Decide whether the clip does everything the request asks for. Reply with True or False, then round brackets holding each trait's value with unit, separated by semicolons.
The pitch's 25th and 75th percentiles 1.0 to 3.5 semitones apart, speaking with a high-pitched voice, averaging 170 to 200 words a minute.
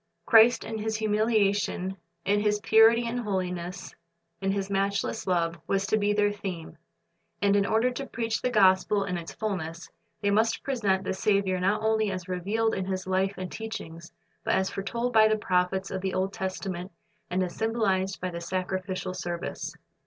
True (2.7 semitones; 195 Hz; 175 wpm)